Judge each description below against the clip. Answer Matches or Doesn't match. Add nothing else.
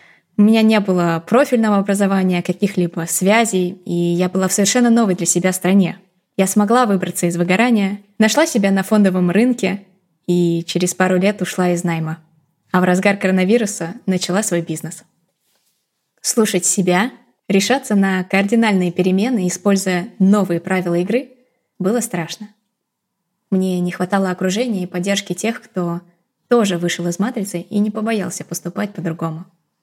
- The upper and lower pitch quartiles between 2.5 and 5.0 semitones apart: Matches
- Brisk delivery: Doesn't match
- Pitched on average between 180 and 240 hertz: Matches